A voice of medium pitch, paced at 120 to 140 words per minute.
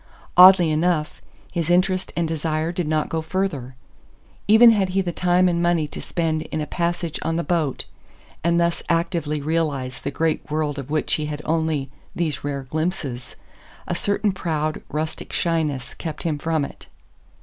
No: medium, 160 Hz; average, 170 wpm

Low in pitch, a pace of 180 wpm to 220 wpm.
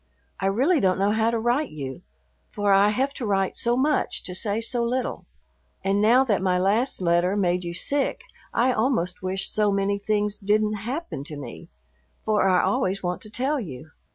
No: high, 205 Hz; average, 190 wpm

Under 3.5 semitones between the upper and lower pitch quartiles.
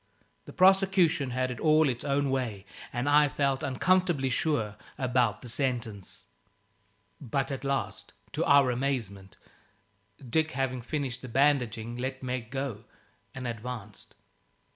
Yes: average, 2.8 semitones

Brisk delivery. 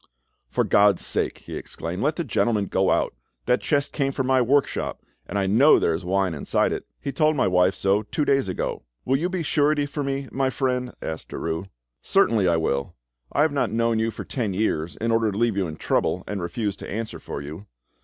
Yes: fast, 220 wpm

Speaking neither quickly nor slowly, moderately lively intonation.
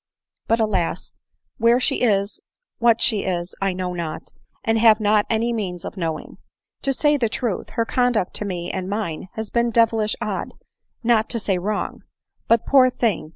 Yes: average, 175 wpm; average, 3.8 semitones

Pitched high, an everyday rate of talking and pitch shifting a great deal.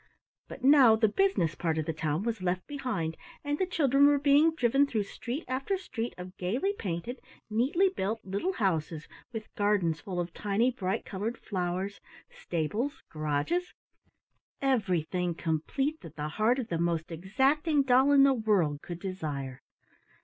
Yes: high, 215 Hz; average, 155 wpm; wide, 8.0 semitones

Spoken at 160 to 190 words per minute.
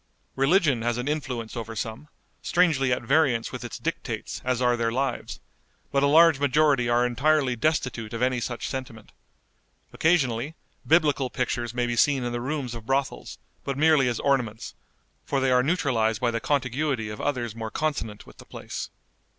Yes: average, 175 wpm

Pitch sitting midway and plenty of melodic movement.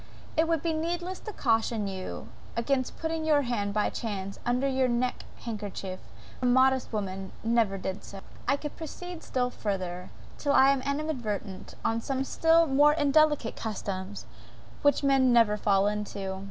No: high, 245 Hz; wide, 5.9 semitones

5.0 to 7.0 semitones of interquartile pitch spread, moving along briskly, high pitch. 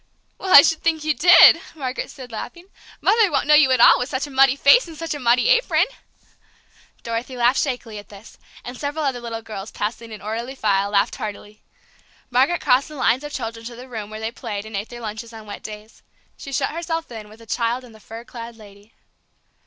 No: average, 4.4 semitones; fast, 220 wpm; high, 240 Hz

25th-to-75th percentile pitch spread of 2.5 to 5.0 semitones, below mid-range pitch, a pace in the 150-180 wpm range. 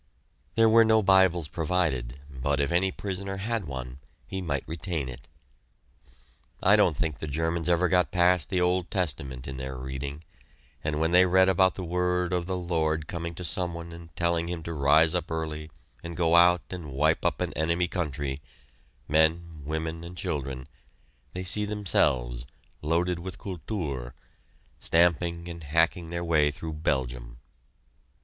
Yes: average, 3.4 semitones; very low, 85 Hz; average, 165 wpm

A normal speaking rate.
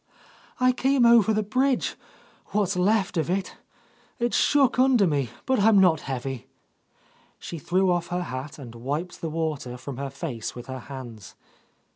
Yes: average, 160 wpm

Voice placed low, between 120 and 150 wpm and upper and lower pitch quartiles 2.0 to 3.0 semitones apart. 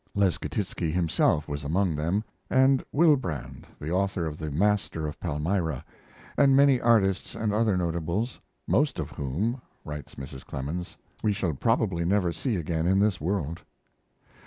No: very low, 90 Hz; average, 145 wpm; average, 5.3 semitones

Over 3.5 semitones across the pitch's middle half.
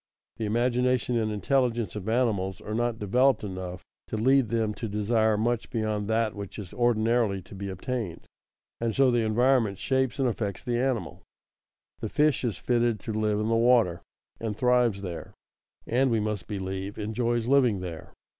No: average, 2.8 semitones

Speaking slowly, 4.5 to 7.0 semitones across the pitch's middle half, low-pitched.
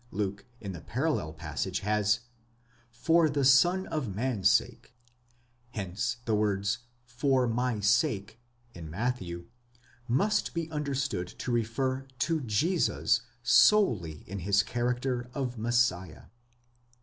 Yes: slow, 115 wpm; average, 5.2 semitones; low, 120 Hz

